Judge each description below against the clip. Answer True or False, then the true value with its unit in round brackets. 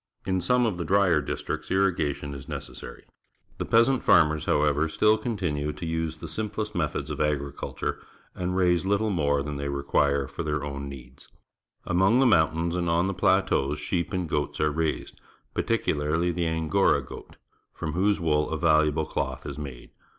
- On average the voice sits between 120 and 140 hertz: False (80 Hz)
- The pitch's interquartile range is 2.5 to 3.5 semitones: False (3.9 semitones)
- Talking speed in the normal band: True (170 wpm)